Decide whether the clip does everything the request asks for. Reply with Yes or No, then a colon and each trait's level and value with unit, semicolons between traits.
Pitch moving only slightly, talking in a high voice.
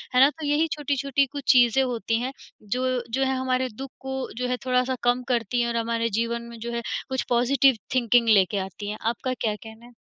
Yes: narrow, 2.2 semitones; high, 245 Hz